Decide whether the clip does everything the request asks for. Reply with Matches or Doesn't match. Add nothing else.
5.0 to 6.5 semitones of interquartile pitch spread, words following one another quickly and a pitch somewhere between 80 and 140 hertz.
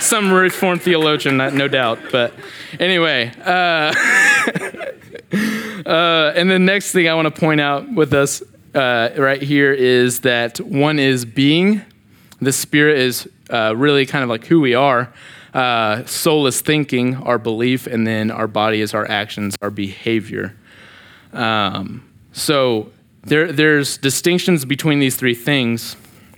Doesn't match